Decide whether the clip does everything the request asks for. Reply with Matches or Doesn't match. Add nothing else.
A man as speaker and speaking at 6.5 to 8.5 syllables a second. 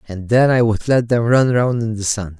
Doesn't match